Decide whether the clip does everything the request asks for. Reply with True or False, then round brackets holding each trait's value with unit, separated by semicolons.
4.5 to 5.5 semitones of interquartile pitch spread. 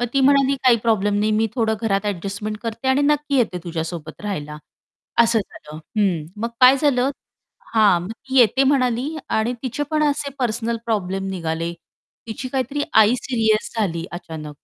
True (5.2 semitones)